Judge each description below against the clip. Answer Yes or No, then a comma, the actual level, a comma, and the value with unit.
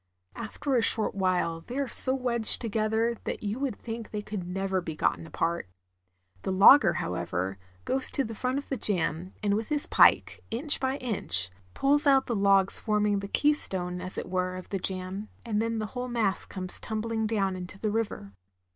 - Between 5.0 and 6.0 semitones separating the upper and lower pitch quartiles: No, average, 4.3 semitones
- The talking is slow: No, average, 190 wpm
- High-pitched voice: Yes, high, 210 Hz